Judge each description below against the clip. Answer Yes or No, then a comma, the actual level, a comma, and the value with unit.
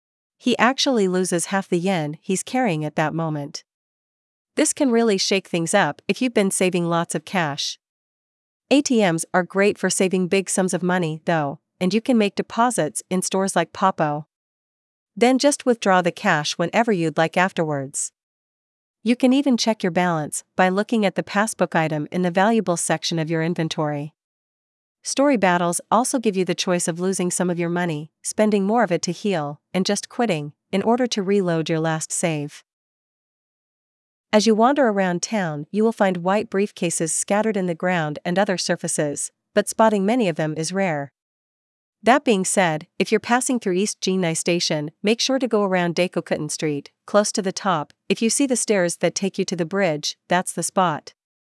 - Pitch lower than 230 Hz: Yes, medium, 185 Hz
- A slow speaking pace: No, average, 185 wpm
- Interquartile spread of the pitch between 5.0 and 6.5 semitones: No, average, 3.9 semitones